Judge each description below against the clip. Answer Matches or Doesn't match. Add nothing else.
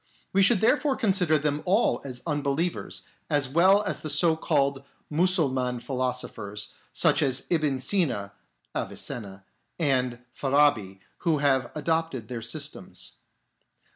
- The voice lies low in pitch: Doesn't match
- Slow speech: Matches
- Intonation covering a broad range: Doesn't match